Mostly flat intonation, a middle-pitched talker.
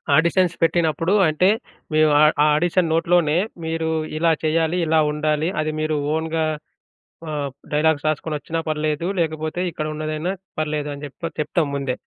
Yes: narrow, 1.4 semitones; medium, 155 Hz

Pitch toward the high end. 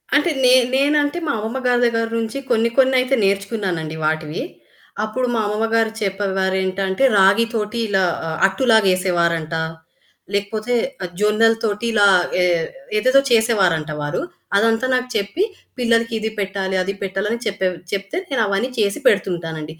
Yes: high, 210 Hz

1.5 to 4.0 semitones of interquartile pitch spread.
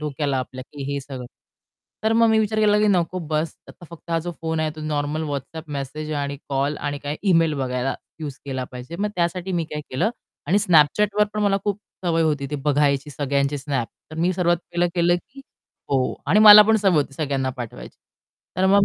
No: average, 4.5 semitones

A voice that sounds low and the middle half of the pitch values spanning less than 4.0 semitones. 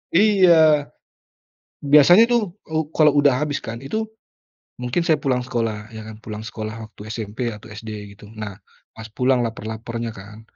No: low, 120 Hz; wide, 5.6 semitones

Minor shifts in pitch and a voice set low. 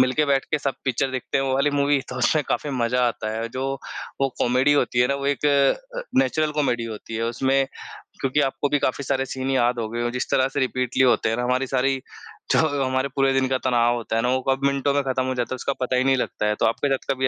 Yes: narrow, 1.9 semitones; low, 130 Hz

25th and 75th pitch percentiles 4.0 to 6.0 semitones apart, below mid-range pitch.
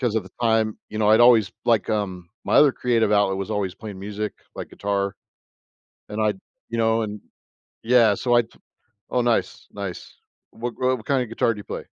No: narrow, 2.4 semitones; low, 110 Hz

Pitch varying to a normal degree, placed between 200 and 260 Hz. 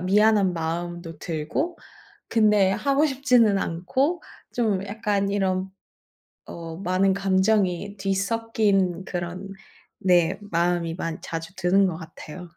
No: average, 3.2 semitones; high, 190 Hz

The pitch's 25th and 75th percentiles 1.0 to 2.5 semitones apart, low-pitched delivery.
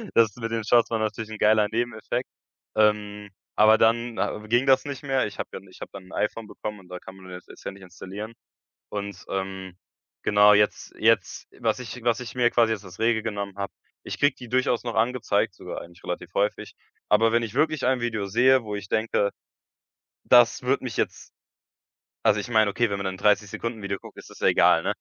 No: average, 2.9 semitones; low, 110 Hz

